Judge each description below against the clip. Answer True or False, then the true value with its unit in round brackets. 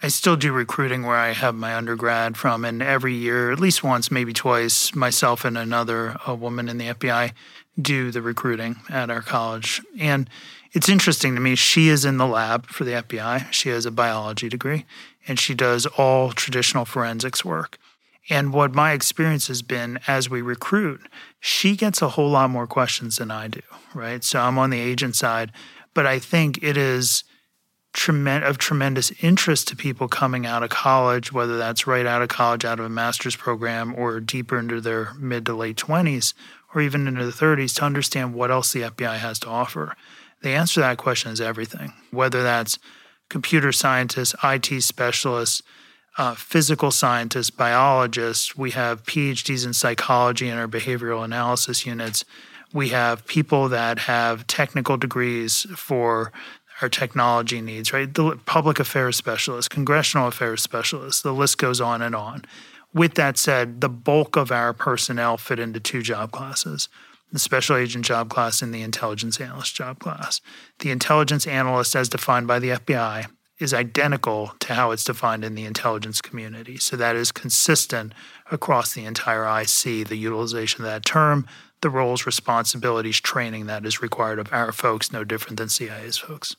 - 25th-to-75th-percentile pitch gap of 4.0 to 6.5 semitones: False (2.9 semitones)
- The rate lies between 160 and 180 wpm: True (175 wpm)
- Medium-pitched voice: False (125 Hz)